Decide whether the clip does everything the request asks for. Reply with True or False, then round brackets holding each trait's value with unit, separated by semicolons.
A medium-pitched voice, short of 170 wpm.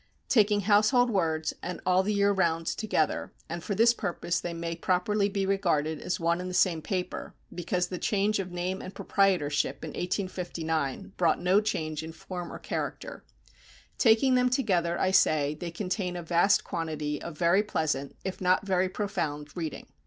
False (180 Hz; 175 wpm)